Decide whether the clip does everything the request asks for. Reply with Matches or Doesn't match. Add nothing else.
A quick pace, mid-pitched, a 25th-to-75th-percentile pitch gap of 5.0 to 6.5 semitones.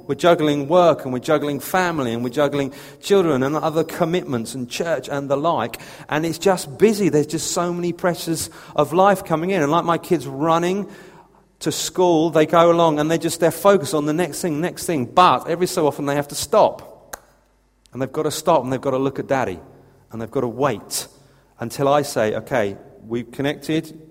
Doesn't match